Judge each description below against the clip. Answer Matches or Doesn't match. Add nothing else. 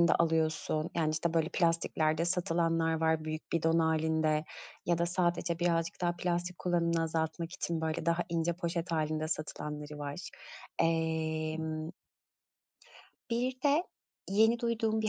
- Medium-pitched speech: Matches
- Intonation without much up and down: Matches